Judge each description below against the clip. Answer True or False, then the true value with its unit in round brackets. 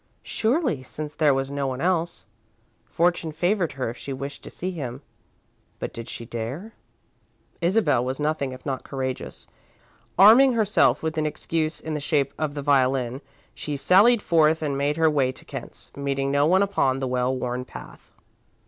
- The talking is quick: False (175 wpm)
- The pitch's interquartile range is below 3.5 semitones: False (4.1 semitones)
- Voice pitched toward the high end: False (145 Hz)